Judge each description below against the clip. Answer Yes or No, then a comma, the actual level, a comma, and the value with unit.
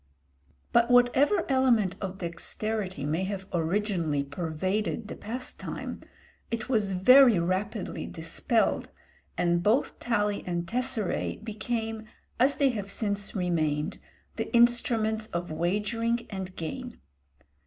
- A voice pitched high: Yes, high, 205 Hz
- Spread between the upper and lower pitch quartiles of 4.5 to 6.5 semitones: Yes, average, 4.8 semitones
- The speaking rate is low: Yes, slow, 110 wpm